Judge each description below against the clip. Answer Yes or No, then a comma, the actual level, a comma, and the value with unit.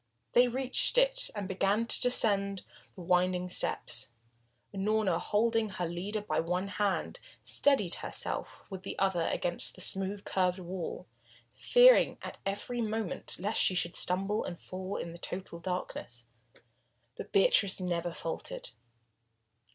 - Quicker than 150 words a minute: No, slow, 135 wpm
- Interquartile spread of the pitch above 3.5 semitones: No, average, 3.1 semitones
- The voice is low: No, high, 190 Hz